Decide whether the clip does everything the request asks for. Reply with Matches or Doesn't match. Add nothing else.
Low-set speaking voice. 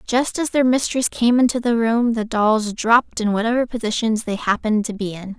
Doesn't match